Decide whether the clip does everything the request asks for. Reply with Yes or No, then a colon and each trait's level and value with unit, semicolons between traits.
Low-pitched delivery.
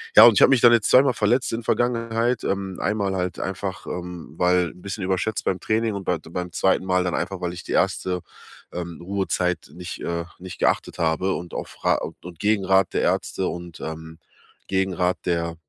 Yes: very low, 95 Hz